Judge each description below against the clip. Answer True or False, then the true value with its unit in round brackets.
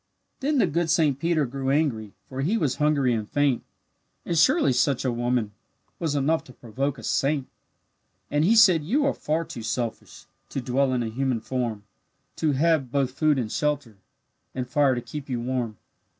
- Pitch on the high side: False (135 Hz)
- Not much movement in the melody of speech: False (3.9 semitones)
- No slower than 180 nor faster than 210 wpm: True (185 wpm)